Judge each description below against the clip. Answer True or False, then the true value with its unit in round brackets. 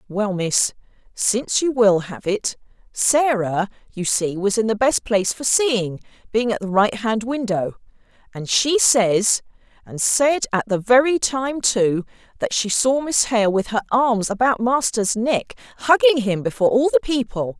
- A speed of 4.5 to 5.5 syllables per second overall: False (4.3 syllables/s)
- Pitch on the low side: False (225 Hz)